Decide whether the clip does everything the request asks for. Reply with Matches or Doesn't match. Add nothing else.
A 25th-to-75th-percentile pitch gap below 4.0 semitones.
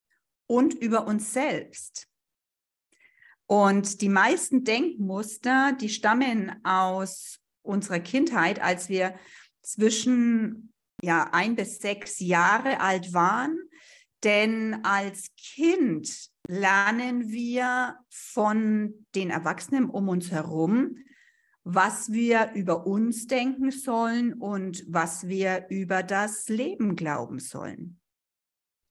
Doesn't match